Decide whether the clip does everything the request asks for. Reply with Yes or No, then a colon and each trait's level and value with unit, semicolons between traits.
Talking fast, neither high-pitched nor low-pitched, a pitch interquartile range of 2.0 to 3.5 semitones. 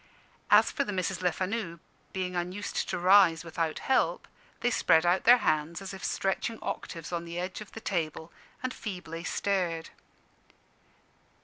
No: average, 150 wpm; medium, 180 Hz; average, 2.8 semitones